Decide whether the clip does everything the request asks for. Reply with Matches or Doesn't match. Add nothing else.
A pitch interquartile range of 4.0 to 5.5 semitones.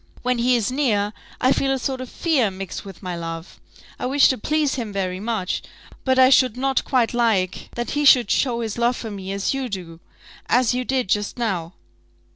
Matches